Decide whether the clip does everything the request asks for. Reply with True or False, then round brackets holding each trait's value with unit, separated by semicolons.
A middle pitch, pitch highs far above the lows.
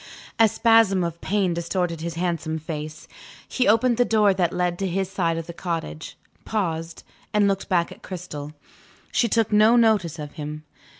False (180 Hz; 4.0 semitones)